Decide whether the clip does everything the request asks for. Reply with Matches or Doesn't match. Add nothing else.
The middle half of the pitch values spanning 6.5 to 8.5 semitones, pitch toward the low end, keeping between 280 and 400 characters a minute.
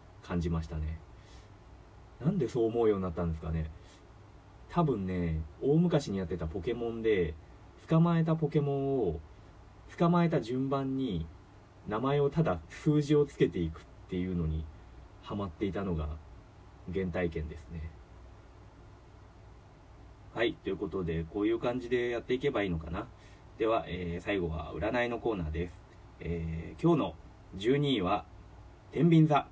Doesn't match